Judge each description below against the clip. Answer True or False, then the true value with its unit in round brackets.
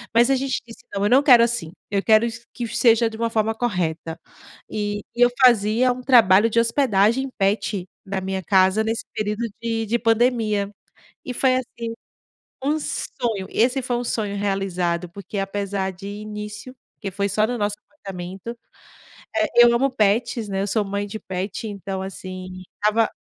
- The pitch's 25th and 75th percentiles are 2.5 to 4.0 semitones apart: True (3.2 semitones)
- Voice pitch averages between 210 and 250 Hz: True (215 Hz)